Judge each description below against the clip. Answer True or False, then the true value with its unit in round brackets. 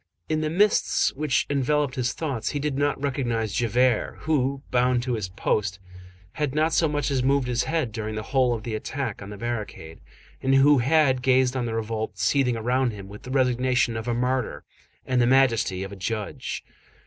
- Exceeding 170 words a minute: True (195 wpm)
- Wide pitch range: False (3.5 semitones)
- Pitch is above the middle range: False (125 Hz)